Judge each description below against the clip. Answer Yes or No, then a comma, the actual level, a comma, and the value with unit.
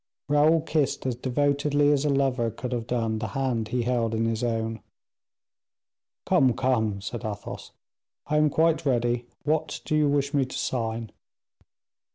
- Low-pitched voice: Yes, low, 125 Hz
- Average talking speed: Yes, average, 160 wpm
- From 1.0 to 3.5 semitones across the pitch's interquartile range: No, average, 4.0 semitones